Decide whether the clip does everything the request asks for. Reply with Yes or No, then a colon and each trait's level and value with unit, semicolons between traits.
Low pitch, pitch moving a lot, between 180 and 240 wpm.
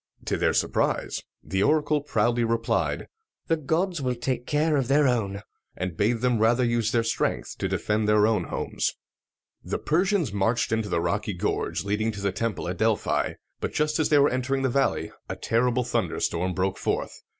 No: low, 120 Hz; average, 4.8 semitones; average, 185 wpm